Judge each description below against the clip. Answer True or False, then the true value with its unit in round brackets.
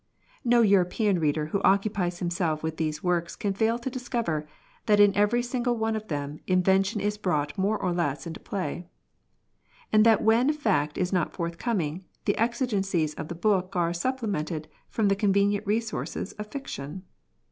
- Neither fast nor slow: True (165 wpm)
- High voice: True (195 Hz)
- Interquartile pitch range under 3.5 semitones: False (4.4 semitones)